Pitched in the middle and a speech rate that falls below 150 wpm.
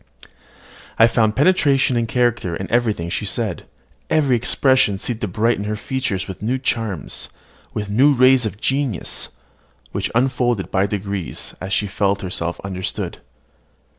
No: low, 110 Hz; average, 140 wpm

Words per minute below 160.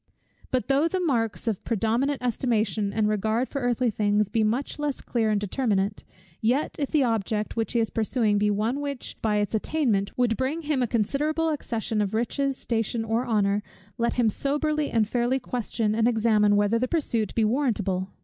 No: average, 185 wpm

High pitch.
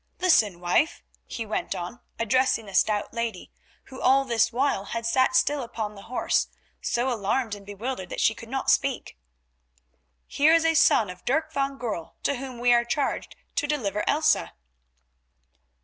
Yes: high, 240 Hz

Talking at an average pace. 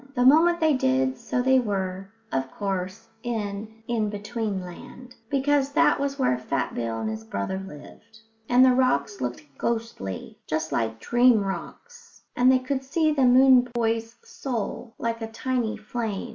Yes: average, 160 wpm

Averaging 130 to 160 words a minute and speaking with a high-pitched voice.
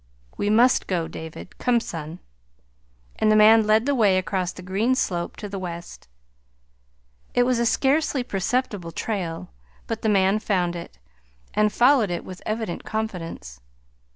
Yes: average, 155 wpm; high, 205 Hz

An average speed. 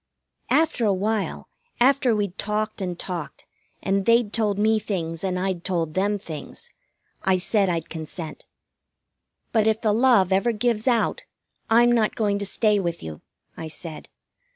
Yes: average, 155 wpm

